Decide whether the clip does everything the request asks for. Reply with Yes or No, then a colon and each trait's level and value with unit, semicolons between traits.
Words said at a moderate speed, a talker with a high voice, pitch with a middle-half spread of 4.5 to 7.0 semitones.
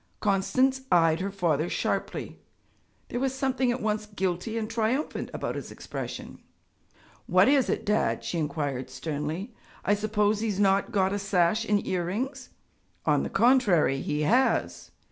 Yes: average, 150 wpm; high, 205 Hz; average, 5.2 semitones